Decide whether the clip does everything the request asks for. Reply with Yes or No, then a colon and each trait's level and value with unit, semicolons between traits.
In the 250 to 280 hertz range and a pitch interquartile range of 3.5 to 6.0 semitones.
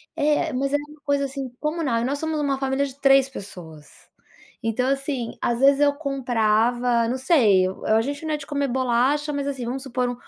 No: very high, 270 Hz; average, 2.9 semitones